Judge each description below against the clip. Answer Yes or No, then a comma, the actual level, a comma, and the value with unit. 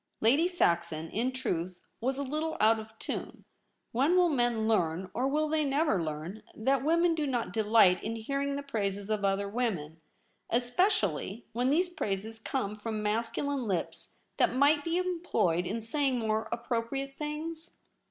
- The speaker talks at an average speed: Yes, average, 160 wpm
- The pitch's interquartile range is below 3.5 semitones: No, average, 5.3 semitones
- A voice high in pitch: Yes, high, 235 Hz